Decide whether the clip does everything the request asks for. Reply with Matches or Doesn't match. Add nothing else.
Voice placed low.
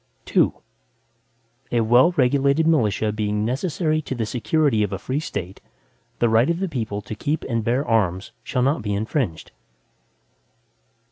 Matches